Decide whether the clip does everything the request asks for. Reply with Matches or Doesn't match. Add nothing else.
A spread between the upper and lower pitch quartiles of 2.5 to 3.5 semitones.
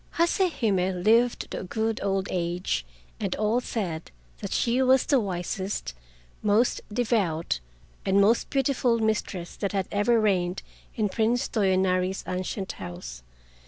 Doesn't match